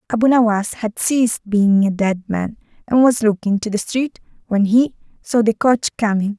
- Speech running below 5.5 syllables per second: Yes, 5.0 syllables/s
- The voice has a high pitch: Yes, high, 220 Hz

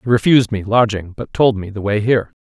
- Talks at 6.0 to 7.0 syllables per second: Yes, 6.3 syllables/s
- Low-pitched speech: Yes, low, 110 Hz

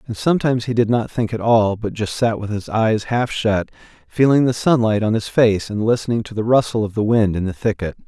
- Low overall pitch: Yes, low, 110 Hz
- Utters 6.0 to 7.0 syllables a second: No, 5.6 syllables/s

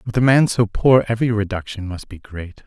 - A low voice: Yes, low, 110 Hz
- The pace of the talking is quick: Yes, fast, 225 wpm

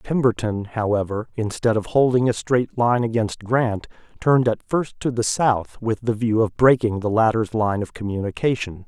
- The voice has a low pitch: Yes, low, 115 Hz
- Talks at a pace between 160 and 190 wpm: Yes, average, 175 wpm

